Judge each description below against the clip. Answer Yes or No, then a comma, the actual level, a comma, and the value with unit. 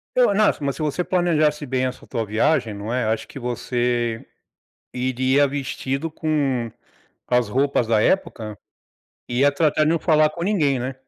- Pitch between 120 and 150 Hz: Yes, low, 135 Hz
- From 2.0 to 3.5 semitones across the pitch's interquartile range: No, average, 4.1 semitones